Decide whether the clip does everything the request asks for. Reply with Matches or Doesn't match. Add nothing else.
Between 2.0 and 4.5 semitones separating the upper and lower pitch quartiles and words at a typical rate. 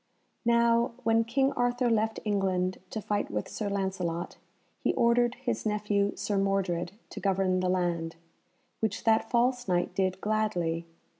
Matches